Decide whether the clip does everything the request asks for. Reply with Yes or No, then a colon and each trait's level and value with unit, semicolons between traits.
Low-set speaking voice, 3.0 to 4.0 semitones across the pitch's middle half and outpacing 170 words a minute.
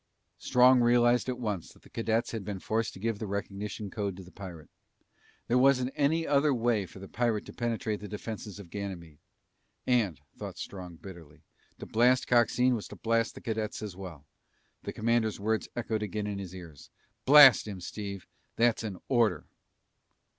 Yes: low, 110 Hz; average, 3.4 semitones; average, 180 wpm